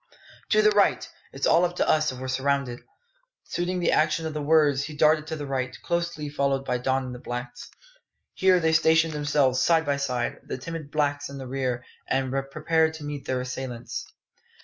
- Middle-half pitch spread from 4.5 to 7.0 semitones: No, average, 3.5 semitones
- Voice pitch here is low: No, medium, 145 Hz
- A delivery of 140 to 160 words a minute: No, average, 195 wpm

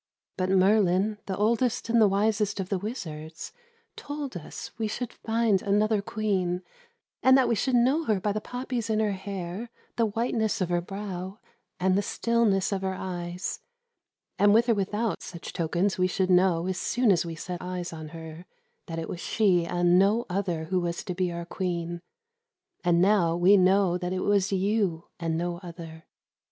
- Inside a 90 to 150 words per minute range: No, average, 185 wpm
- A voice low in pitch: No, high, 190 Hz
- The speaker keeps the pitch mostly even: No, average, 3.4 semitones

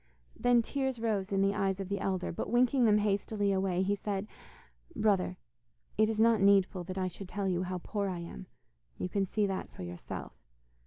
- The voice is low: No, high, 195 Hz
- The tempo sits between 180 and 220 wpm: Yes, average, 200 wpm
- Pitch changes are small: Yes, narrow, 2.2 semitones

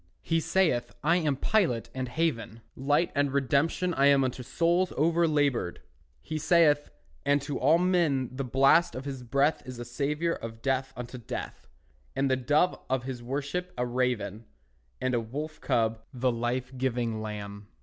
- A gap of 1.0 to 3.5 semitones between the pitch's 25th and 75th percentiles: No, average, 4.0 semitones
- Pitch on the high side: No, low, 135 Hz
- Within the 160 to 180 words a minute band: Yes, average, 165 wpm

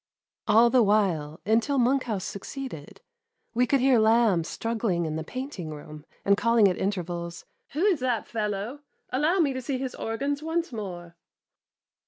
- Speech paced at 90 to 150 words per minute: No, average, 170 wpm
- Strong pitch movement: Yes, wide, 6.2 semitones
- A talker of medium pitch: No, high, 225 Hz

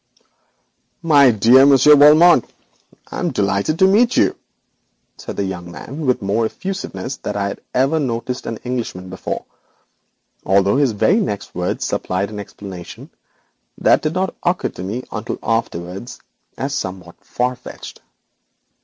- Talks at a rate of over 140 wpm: Yes, average, 150 wpm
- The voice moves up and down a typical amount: No, wide, 6.7 semitones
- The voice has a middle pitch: No, low, 120 Hz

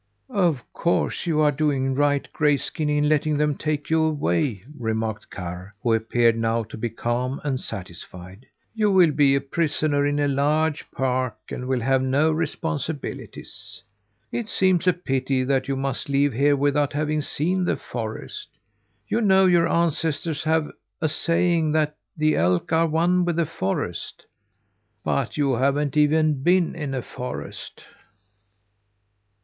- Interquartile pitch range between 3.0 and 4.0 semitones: Yes, average, 3.6 semitones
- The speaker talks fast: No, average, 150 wpm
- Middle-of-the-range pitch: Yes, medium, 145 Hz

